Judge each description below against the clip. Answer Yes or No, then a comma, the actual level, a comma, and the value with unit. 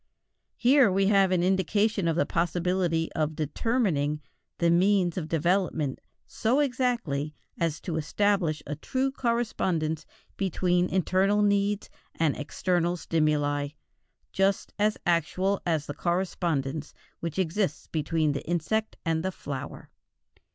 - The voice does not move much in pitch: No, average, 4.1 semitones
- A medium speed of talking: No, slow, 125 wpm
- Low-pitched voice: No, medium, 175 Hz